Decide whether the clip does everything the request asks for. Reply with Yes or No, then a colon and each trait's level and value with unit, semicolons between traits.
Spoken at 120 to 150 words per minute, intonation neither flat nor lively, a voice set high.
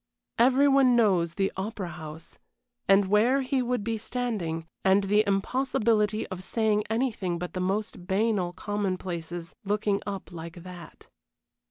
Yes: average, 140 wpm; average, 3.8 semitones; high, 200 Hz